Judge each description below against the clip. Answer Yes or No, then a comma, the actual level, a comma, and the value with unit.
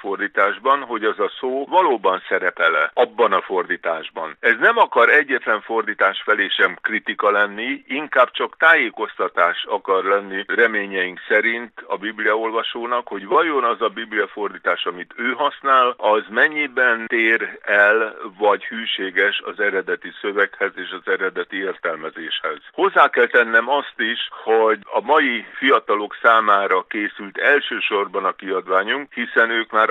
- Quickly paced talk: No, average, 135 wpm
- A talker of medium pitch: No, low, 130 Hz